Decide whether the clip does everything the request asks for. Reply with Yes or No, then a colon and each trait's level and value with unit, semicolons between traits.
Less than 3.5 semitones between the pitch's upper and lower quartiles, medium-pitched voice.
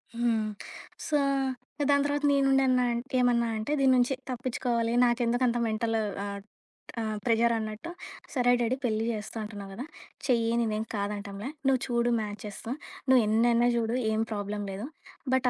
No: narrow, 2.5 semitones; high, 235 Hz